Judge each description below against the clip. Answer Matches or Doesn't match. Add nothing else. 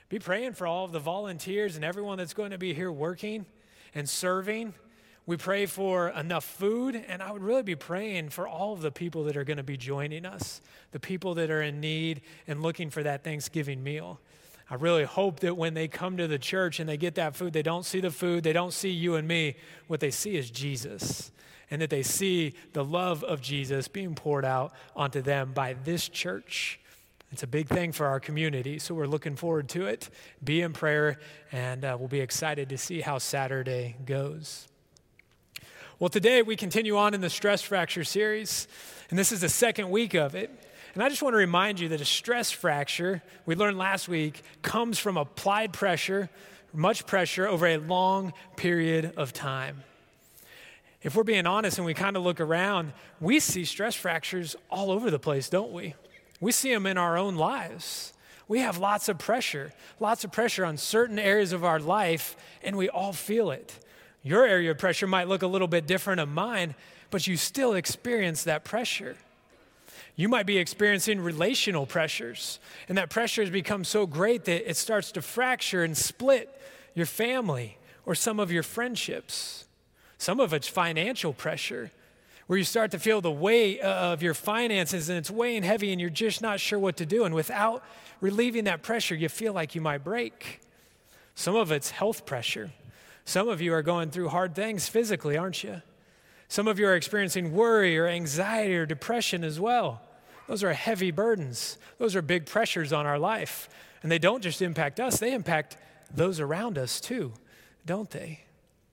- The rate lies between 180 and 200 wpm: Matches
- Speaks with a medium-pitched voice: Matches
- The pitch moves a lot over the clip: Doesn't match